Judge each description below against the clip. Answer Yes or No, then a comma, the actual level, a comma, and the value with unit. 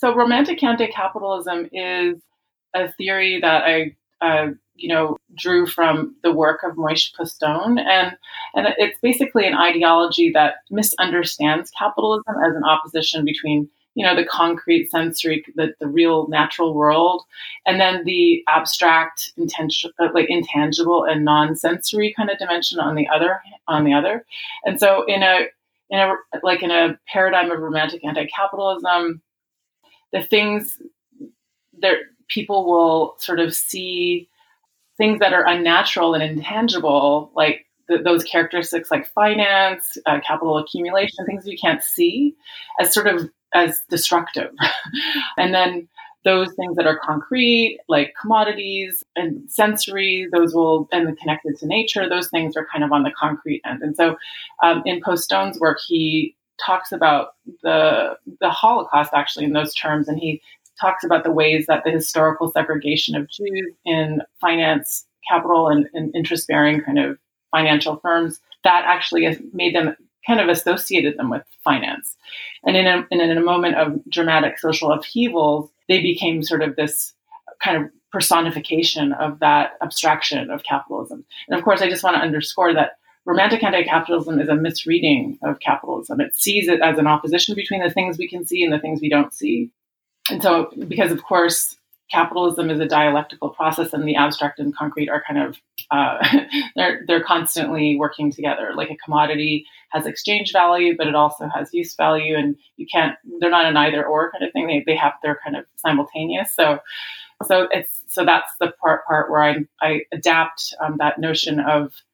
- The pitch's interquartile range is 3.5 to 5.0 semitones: Yes, average, 3.8 semitones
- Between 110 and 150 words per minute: No, average, 165 wpm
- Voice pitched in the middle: Yes, medium, 170 Hz